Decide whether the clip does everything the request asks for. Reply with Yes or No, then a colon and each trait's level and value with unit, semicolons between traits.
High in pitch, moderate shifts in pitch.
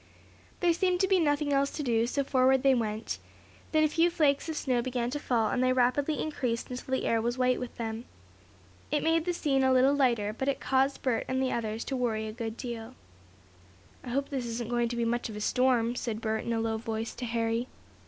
Yes: very high, 250 Hz; average, 3.2 semitones